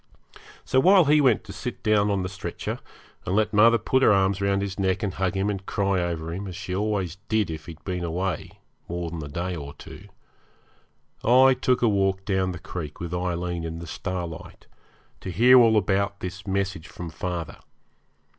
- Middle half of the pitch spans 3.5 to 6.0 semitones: No, average, 3.1 semitones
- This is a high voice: No, very low, 95 Hz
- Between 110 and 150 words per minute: No, average, 195 wpm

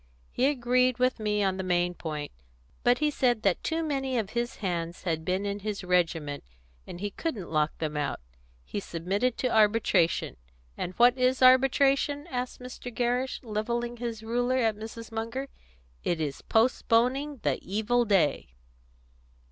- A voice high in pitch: Yes, high, 225 Hz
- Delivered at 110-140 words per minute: No, average, 155 wpm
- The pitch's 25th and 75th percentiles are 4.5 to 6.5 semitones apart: Yes, average, 5.3 semitones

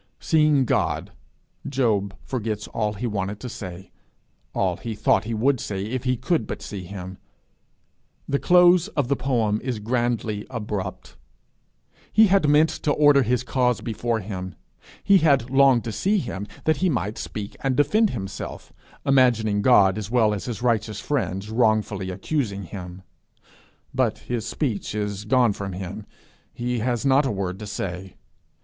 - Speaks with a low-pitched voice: Yes, low, 115 Hz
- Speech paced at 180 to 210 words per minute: No, average, 160 wpm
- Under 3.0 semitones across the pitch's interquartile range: No, average, 4.6 semitones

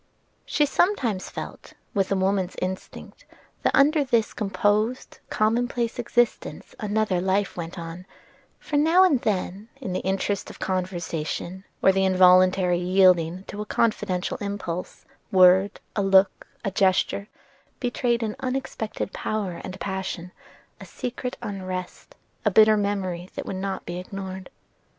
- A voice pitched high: Yes, high, 195 Hz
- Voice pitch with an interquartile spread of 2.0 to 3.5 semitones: Yes, average, 2.9 semitones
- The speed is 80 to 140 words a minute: Yes, slow, 135 wpm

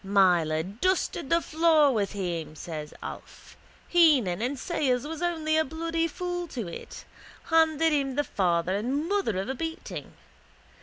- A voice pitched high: Yes, very high, 280 Hz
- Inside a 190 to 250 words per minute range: No, average, 150 wpm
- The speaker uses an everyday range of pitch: No, wide, 9.0 semitones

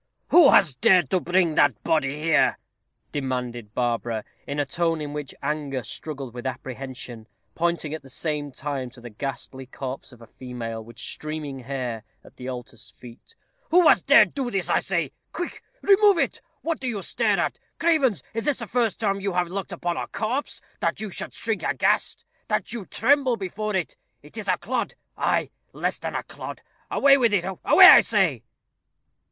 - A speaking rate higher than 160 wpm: Yes, average, 185 wpm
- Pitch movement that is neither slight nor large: No, wide, 8.5 semitones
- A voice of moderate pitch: Yes, medium, 155 Hz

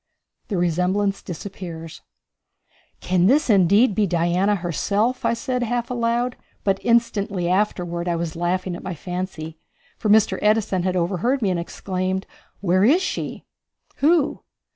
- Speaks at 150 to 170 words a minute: No, average, 140 wpm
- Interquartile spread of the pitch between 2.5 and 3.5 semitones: No, average, 4.1 semitones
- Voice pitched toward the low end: No, high, 190 Hz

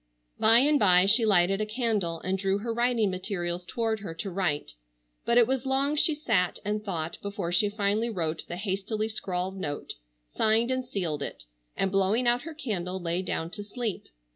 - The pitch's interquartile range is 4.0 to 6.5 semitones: Yes, average, 4.3 semitones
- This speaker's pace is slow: No, average, 190 wpm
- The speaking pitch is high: Yes, high, 200 Hz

